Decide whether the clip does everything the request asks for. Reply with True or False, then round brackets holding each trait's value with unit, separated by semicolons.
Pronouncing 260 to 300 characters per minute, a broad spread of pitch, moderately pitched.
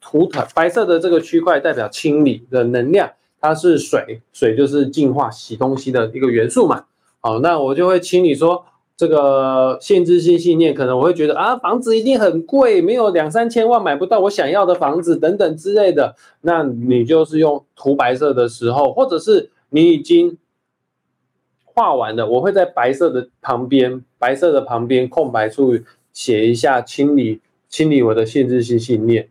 True (270 characters per minute; 6.0 semitones; 150 Hz)